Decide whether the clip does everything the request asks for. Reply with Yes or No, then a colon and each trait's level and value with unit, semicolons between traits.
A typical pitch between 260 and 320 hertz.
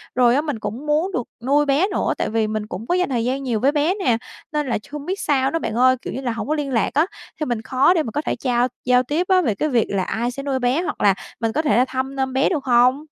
Yes: very high, 265 Hz